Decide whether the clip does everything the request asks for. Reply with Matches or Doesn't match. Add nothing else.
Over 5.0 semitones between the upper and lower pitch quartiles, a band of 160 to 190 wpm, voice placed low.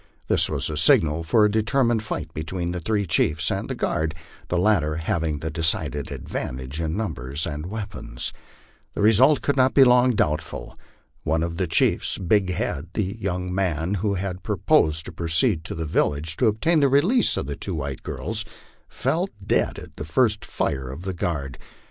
Matches